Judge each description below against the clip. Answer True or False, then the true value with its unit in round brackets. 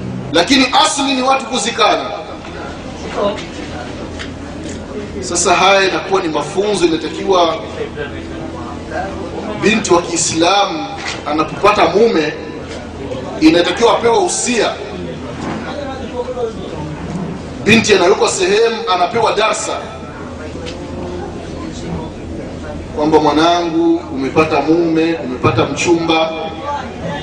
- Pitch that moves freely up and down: True (7.5 semitones)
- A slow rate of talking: True (65 wpm)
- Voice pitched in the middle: True (170 Hz)